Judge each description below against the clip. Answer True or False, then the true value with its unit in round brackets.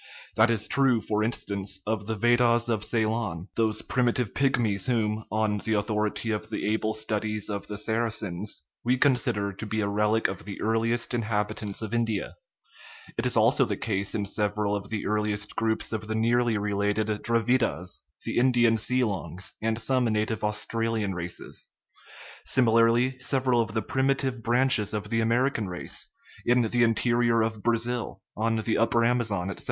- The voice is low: True (110 Hz)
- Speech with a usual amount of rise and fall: False (2.2 semitones)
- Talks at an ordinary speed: True (175 wpm)